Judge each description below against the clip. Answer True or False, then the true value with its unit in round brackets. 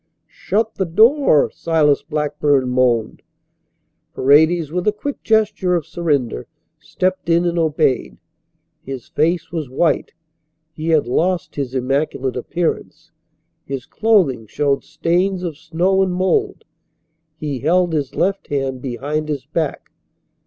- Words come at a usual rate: False (125 wpm)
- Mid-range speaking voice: True (160 Hz)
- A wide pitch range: False (4.6 semitones)